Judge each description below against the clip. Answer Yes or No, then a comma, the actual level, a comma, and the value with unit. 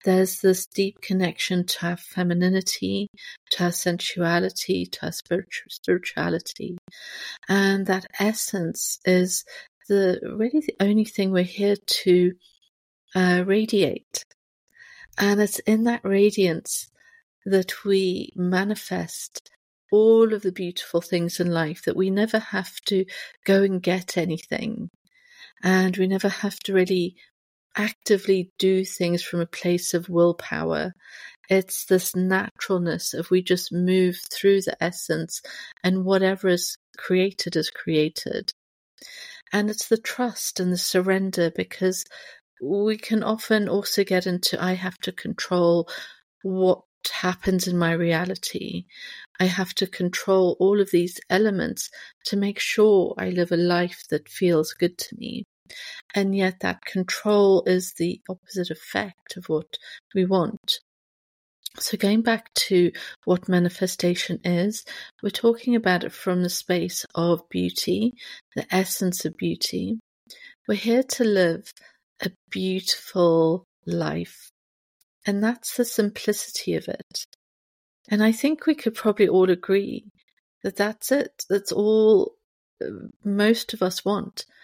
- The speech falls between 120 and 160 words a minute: Yes, slow, 135 wpm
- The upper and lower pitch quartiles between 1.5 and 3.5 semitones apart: Yes, average, 2.7 semitones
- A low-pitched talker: No, high, 190 Hz